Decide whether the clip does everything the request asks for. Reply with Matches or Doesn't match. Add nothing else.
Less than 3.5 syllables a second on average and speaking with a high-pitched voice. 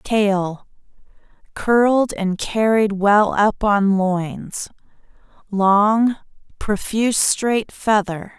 Matches